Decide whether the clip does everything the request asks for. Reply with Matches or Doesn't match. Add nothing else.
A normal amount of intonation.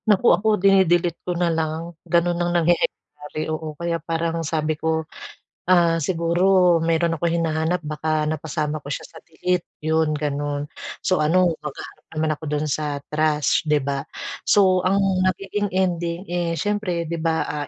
Doesn't match